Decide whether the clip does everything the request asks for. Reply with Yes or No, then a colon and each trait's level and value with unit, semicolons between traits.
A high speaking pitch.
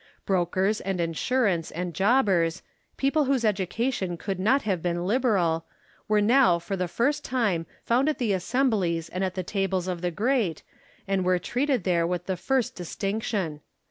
Yes: high, 195 Hz